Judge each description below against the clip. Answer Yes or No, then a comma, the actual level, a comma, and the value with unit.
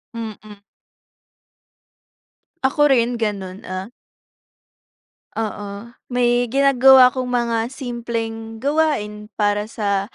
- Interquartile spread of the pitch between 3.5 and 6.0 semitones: No, average, 3.1 semitones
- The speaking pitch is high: Yes, high, 230 Hz